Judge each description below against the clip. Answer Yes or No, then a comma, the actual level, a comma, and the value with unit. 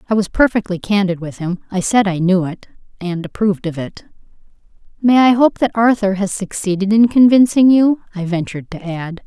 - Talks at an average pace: Yes, average, 180 wpm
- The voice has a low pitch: No, high, 200 Hz